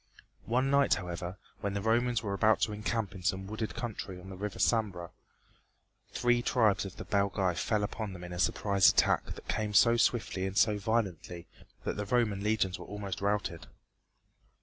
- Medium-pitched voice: No, low, 105 Hz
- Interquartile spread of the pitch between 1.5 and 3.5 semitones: Yes, average, 2.8 semitones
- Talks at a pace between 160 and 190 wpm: Yes, average, 180 wpm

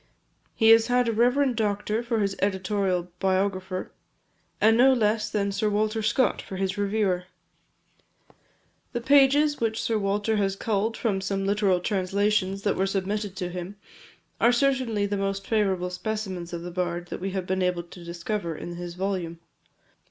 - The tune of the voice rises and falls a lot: No, average, 2.9 semitones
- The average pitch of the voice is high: Yes, high, 200 Hz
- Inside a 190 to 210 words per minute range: No, average, 165 wpm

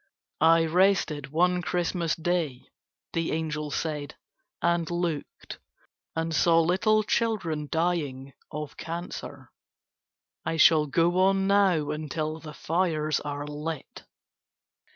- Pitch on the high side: No, medium, 165 Hz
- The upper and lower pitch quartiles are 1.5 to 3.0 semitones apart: Yes, narrow, 2.6 semitones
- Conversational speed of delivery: No, slow, 110 wpm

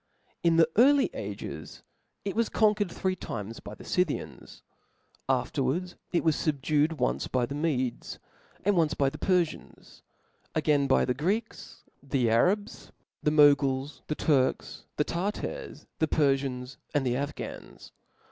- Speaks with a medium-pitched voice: Yes, medium, 150 Hz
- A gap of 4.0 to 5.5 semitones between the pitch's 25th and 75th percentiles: Yes, average, 5.1 semitones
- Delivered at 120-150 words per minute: Yes, average, 140 wpm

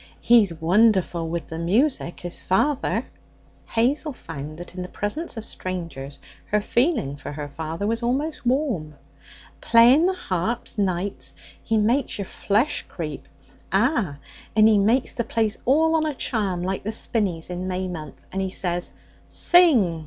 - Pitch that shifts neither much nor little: No, wide, 5.8 semitones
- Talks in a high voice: Yes, high, 205 Hz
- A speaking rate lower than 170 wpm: Yes, average, 155 wpm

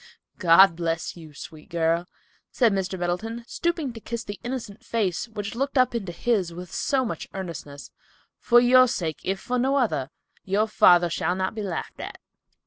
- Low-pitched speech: No, high, 195 Hz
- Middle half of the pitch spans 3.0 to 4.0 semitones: No, wide, 5.5 semitones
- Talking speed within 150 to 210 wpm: Yes, average, 175 wpm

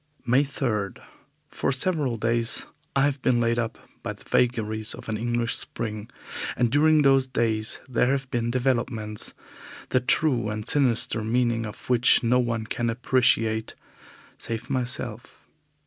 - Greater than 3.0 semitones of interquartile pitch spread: No, narrow, 2.4 semitones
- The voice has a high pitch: No, low, 120 Hz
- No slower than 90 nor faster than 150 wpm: Yes, average, 145 wpm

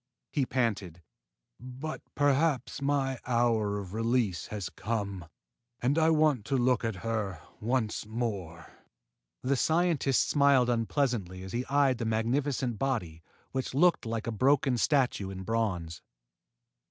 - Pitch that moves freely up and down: No, average, 4.6 semitones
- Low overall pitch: Yes, low, 120 Hz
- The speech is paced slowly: Yes, slow, 130 wpm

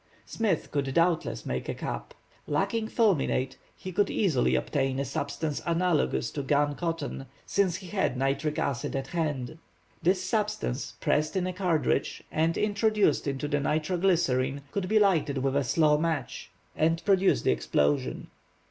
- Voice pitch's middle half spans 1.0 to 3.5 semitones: No, average, 5.2 semitones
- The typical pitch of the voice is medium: Yes, medium, 155 Hz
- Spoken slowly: No, average, 155 wpm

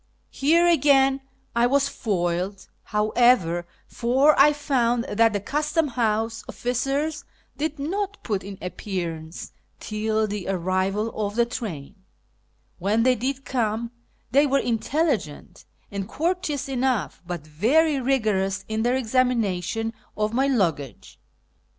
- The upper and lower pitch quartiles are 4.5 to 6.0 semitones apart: Yes, wide, 5.4 semitones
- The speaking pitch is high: Yes, high, 230 Hz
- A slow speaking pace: Yes, slow, 120 wpm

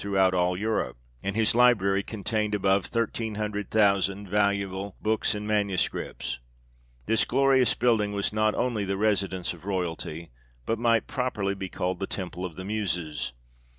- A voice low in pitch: Yes, low, 100 Hz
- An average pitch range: No, narrow, 2.3 semitones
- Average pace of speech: Yes, average, 155 wpm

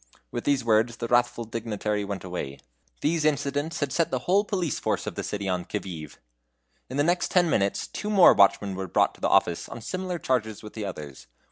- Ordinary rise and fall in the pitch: No, wide, 7.3 semitones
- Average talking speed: No, fast, 220 wpm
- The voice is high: No, low, 115 Hz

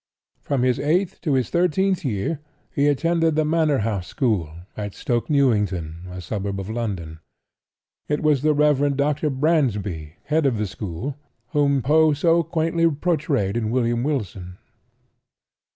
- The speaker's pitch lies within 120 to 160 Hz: Yes, medium, 140 Hz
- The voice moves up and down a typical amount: No, wide, 6.8 semitones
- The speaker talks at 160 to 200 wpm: No, average, 145 wpm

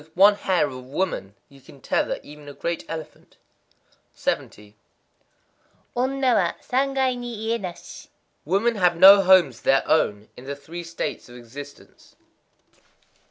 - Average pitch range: No, wide, 6.8 semitones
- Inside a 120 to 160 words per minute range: Yes, average, 150 wpm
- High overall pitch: No, medium, 170 Hz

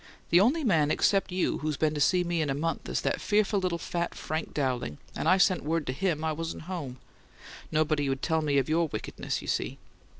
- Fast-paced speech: Yes, fast, 220 wpm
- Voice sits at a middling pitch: Yes, medium, 160 Hz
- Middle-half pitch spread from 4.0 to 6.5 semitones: No, average, 3.5 semitones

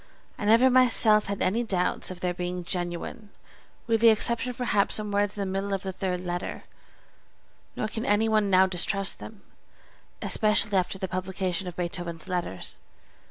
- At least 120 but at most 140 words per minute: No, average, 170 wpm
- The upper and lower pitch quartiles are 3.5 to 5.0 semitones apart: No, average, 2.9 semitones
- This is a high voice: Yes, high, 195 Hz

